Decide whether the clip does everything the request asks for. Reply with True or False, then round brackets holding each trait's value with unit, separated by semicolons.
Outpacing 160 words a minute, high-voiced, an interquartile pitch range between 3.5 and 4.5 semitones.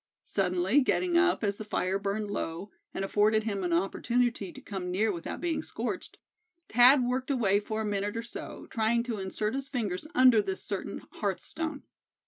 True (180 wpm; 215 Hz; 4.0 semitones)